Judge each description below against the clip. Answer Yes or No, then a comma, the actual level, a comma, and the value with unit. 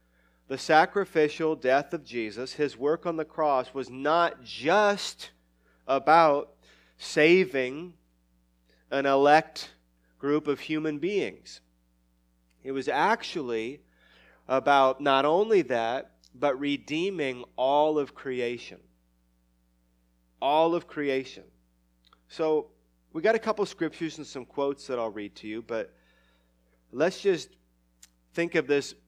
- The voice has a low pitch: Yes, low, 130 Hz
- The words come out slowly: Yes, slow, 120 wpm